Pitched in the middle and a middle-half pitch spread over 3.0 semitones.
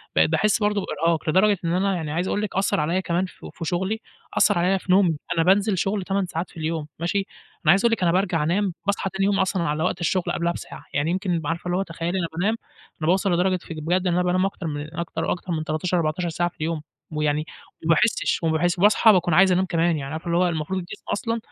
No: medium, 175 Hz; narrow, 2.6 semitones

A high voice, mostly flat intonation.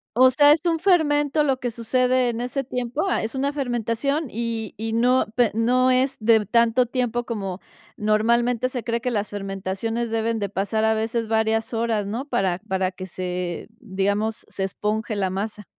No: high, 230 Hz; average, 3.2 semitones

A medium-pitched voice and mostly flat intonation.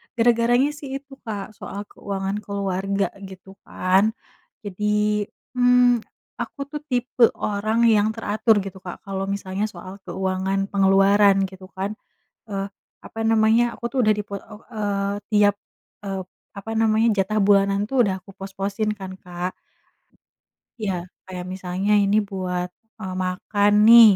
No: high, 200 Hz; narrow, 2.1 semitones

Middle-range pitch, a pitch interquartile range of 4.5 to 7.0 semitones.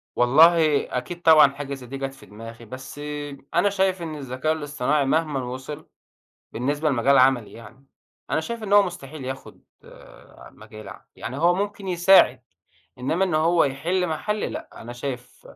Yes: medium, 145 Hz; average, 4.8 semitones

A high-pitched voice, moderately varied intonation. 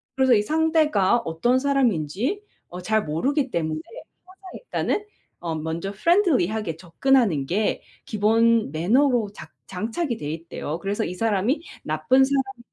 No: high, 220 Hz; wide, 7.9 semitones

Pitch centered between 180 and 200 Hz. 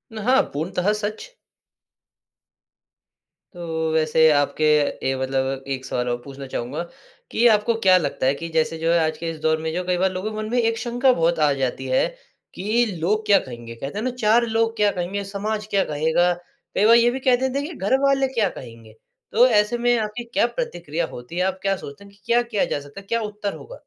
Yes: high, 190 Hz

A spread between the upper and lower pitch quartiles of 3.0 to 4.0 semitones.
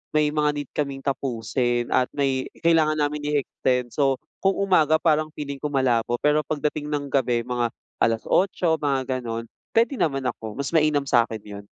Yes: average, 3.4 semitones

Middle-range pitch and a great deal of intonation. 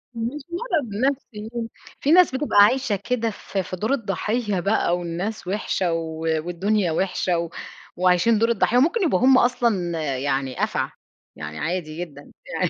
No: high, 205 Hz; wide, 5.9 semitones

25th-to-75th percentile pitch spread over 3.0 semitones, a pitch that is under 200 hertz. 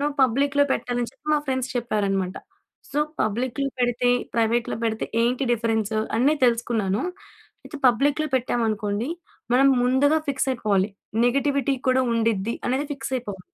No: average, 3.6 semitones; high, 245 Hz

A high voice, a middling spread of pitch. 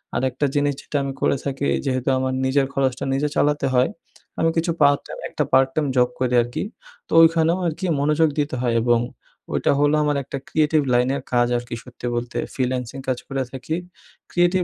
No: low, 135 Hz; average, 3.0 semitones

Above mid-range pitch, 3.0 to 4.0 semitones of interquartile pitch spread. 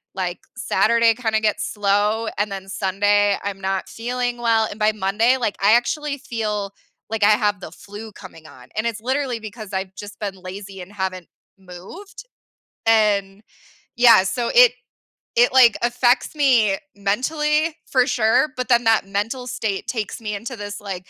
Yes: high, 215 Hz; average, 3.4 semitones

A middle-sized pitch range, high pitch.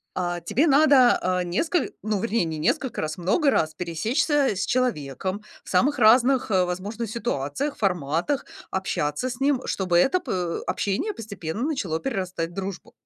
No: wide, 6.8 semitones; high, 200 Hz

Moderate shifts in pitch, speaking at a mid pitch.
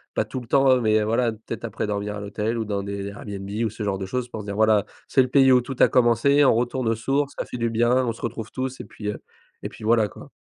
No: average, 3.3 semitones; low, 115 Hz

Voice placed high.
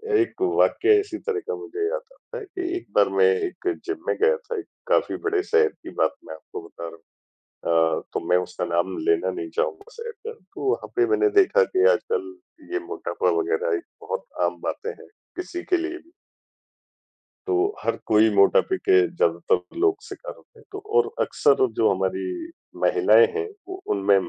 Yes: very high, 400 Hz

